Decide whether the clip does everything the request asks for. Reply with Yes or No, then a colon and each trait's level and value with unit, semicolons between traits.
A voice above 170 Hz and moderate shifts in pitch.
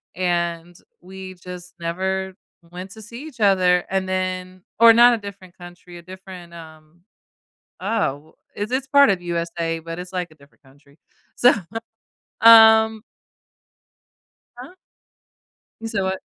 Yes: medium, 185 Hz; average, 3.1 semitones